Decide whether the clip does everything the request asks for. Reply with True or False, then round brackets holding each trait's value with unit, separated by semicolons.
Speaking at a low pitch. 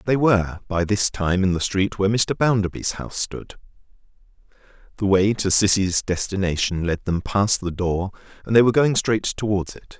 True (100 Hz)